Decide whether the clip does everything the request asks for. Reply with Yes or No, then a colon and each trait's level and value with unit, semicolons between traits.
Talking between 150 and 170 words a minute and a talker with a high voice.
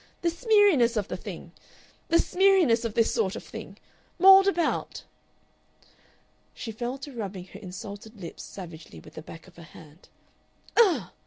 Yes: average, 155 wpm; high, 230 Hz